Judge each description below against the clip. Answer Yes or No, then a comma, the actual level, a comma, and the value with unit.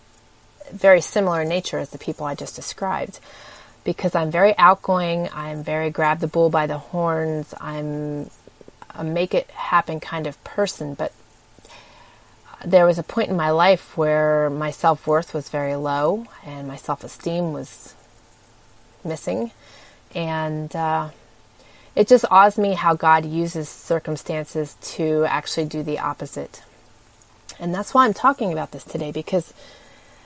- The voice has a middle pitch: Yes, medium, 155 Hz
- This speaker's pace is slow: No, average, 145 wpm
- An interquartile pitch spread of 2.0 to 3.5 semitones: Yes, average, 2.9 semitones